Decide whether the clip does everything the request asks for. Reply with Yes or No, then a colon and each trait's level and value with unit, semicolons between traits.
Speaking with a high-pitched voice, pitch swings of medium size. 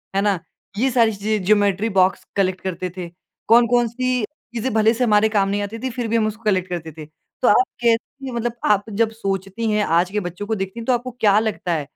Yes: high, 215 Hz; average, 3.0 semitones